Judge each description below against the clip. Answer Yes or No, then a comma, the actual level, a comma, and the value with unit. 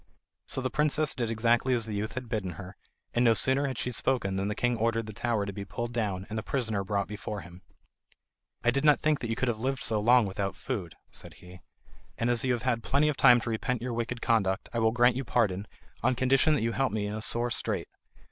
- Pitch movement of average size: Yes, average, 3.3 semitones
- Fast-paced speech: Yes, fast, 250 wpm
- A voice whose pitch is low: Yes, low, 115 Hz